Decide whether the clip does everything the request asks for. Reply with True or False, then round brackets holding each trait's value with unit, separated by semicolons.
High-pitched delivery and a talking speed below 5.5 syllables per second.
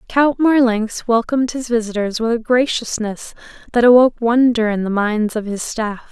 True (230 Hz; 5.0 syllables/s)